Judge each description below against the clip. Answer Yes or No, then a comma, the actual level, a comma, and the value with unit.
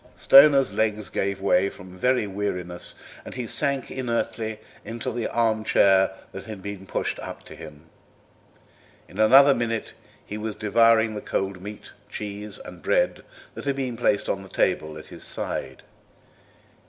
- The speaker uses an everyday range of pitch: Yes, average, 3.3 semitones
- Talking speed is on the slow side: No, average, 155 wpm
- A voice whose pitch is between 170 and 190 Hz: No, low, 105 Hz